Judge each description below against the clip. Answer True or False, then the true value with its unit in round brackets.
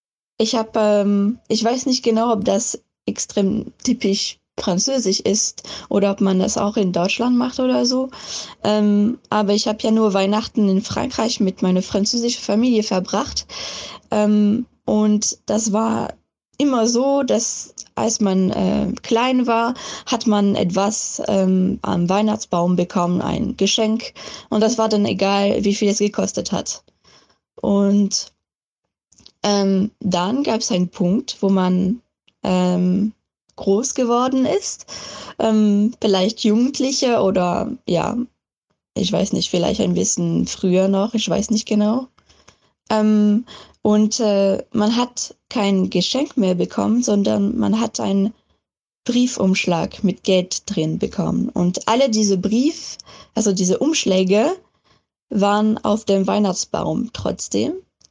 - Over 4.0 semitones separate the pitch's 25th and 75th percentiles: False (2.7 semitones)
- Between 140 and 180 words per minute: False (130 wpm)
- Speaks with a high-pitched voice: True (210 Hz)